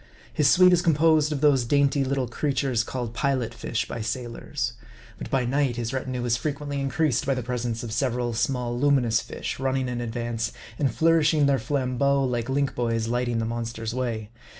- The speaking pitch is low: Yes, low, 130 Hz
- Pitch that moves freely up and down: No, average, 3.0 semitones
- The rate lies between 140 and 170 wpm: No, average, 190 wpm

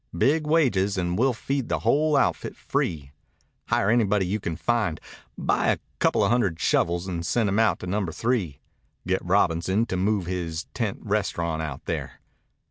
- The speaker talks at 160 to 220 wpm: Yes, average, 165 wpm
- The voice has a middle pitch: No, very low, 95 Hz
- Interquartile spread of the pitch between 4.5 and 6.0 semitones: Yes, average, 5.1 semitones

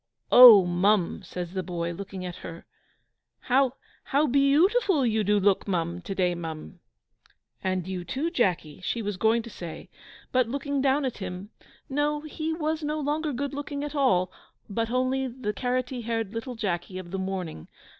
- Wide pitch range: Yes, wide, 7.0 semitones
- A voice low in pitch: No, high, 225 Hz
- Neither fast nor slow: Yes, average, 170 wpm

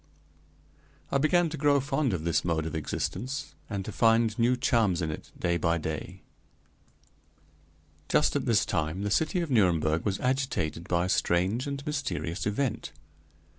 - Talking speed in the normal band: Yes, average, 160 wpm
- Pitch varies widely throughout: Yes, wide, 8.1 semitones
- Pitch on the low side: Yes, low, 105 Hz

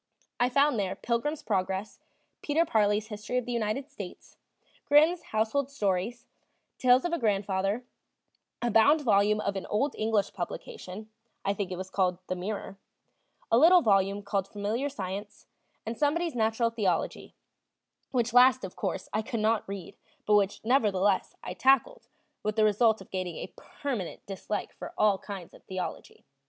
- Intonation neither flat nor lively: Yes, average, 4.1 semitones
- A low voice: No, high, 215 Hz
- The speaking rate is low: No, average, 160 wpm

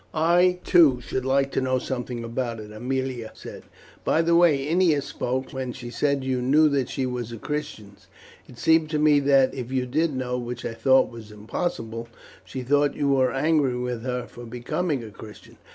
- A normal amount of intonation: Yes, average, 3.2 semitones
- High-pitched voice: No, low, 130 Hz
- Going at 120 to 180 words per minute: No, average, 195 wpm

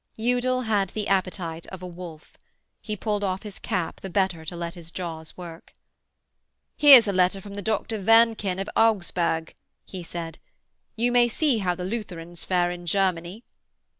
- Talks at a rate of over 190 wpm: No, average, 165 wpm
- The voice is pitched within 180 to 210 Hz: Yes, high, 190 Hz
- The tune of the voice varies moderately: Yes, average, 3.9 semitones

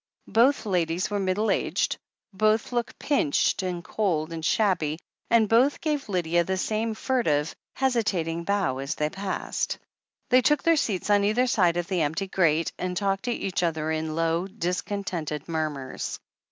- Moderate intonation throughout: Yes, average, 4.9 semitones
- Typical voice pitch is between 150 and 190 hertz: Yes, medium, 185 Hz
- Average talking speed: Yes, average, 160 wpm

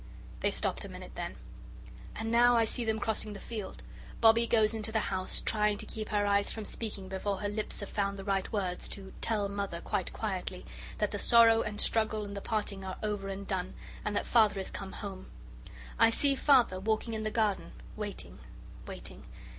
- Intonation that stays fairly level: Yes, narrow, 2.1 semitones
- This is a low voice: No, high, 210 Hz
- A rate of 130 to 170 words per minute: No, average, 200 wpm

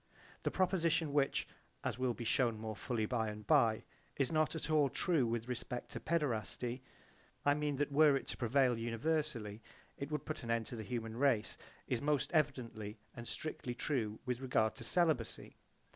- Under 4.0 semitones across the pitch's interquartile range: No, average, 4.5 semitones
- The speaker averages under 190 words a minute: Yes, average, 180 wpm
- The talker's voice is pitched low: Yes, low, 125 Hz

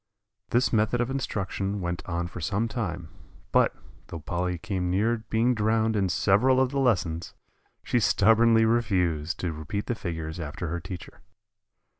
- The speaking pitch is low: Yes, low, 100 Hz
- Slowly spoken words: No, average, 155 wpm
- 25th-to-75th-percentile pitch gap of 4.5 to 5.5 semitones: Yes, average, 4.8 semitones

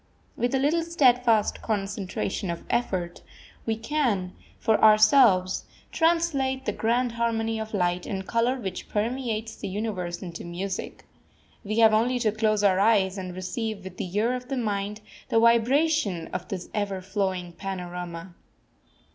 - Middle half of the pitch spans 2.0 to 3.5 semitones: No, average, 4.0 semitones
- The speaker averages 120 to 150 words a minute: Yes, average, 145 wpm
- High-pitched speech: Yes, high, 215 Hz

